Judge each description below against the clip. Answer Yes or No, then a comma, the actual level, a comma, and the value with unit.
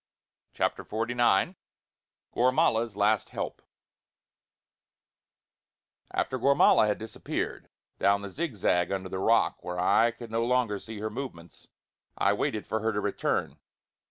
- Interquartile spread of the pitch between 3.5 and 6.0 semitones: No, average, 2.9 semitones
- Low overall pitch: Yes, low, 110 Hz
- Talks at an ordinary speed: No, slow, 120 wpm